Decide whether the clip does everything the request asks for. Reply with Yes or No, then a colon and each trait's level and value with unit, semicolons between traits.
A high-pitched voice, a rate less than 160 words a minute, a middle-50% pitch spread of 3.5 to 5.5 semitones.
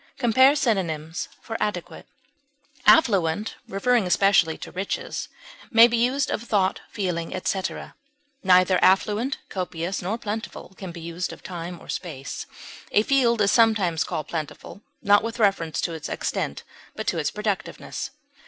Yes: high, 195 Hz; average, 145 wpm; average, 4.7 semitones